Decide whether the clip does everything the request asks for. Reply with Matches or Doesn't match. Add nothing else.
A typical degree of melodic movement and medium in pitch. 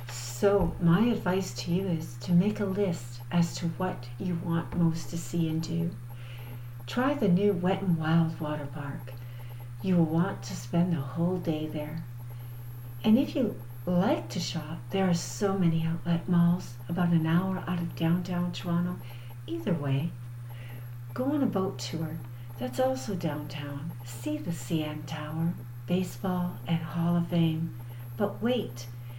Doesn't match